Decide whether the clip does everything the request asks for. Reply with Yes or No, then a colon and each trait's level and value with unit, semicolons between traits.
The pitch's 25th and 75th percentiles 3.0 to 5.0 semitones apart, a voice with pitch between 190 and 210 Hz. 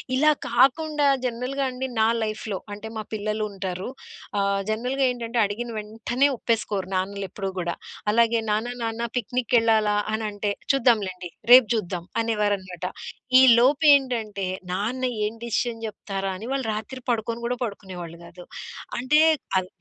No: average, 3.6 semitones; high, 220 Hz